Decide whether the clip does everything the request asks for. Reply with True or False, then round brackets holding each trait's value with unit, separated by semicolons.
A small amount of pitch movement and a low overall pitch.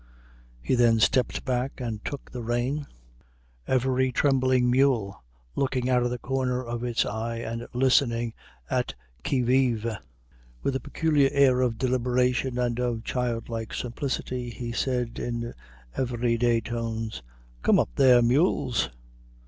True (1.7 semitones; 125 Hz)